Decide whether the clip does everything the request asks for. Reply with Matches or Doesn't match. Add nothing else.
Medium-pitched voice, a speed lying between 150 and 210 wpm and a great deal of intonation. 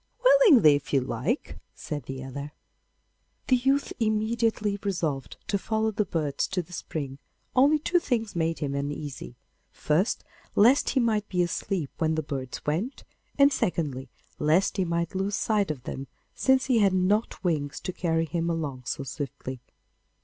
Matches